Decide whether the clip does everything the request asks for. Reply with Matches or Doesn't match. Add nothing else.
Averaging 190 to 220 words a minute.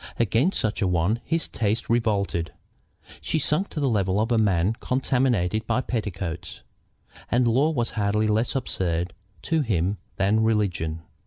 Doesn't match